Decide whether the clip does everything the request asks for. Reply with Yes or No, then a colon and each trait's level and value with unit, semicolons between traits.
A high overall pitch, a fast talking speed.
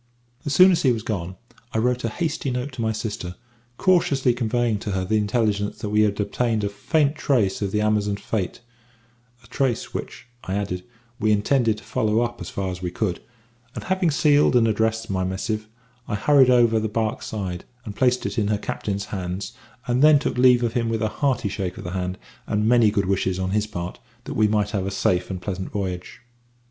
No: low, 110 Hz; fast, 215 wpm